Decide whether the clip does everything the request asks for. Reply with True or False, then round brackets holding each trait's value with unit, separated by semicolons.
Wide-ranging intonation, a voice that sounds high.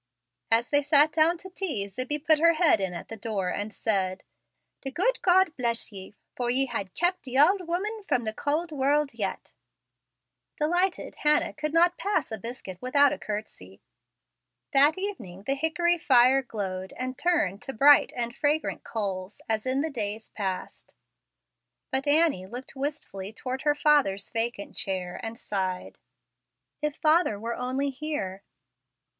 True (6.5 semitones; 265 Hz)